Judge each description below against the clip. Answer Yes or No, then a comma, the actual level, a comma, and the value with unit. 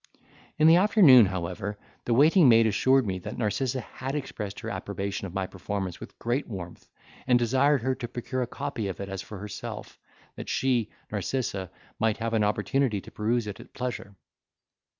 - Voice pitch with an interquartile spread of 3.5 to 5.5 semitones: Yes, average, 4.7 semitones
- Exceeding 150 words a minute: Yes, average, 180 wpm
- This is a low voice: Yes, low, 115 Hz